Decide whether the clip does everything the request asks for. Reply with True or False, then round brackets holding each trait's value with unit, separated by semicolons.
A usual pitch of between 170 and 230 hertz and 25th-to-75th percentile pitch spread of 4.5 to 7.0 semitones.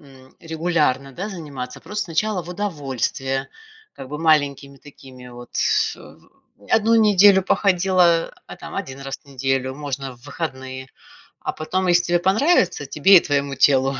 False (150 Hz; 5.2 semitones)